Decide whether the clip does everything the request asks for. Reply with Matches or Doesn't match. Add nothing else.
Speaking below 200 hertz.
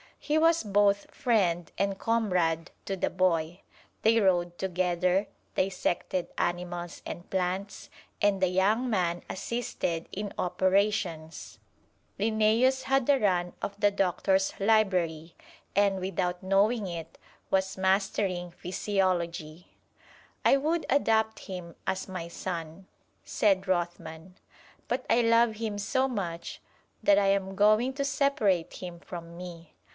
Matches